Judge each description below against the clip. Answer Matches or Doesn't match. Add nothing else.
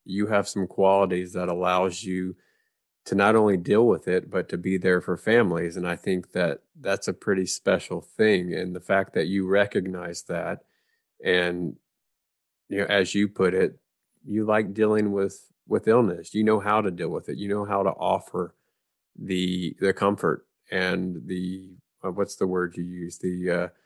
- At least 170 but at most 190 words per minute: Matches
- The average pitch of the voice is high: Doesn't match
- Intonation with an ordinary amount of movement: Doesn't match